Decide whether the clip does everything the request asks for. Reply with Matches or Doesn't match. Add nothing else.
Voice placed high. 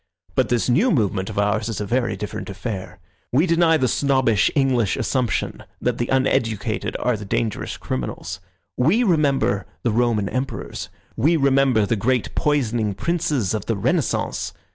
Doesn't match